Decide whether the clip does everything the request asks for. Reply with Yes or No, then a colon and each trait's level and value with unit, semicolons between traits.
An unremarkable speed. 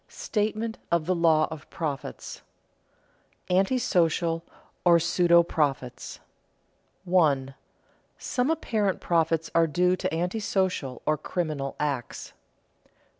No: slow, 100 wpm